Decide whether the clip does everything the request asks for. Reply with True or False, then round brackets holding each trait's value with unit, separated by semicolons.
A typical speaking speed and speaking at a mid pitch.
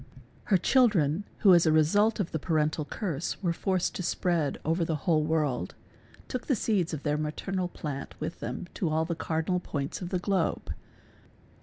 True (185 wpm; 165 Hz)